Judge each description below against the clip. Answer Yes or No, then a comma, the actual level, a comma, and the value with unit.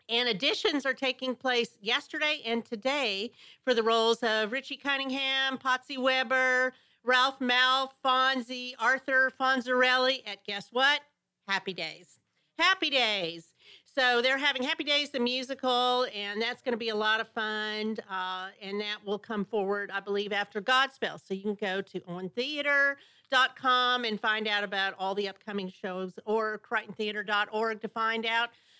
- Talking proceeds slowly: No, average, 150 wpm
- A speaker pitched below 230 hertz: No, high, 235 Hz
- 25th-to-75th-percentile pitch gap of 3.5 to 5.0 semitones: Yes, average, 3.9 semitones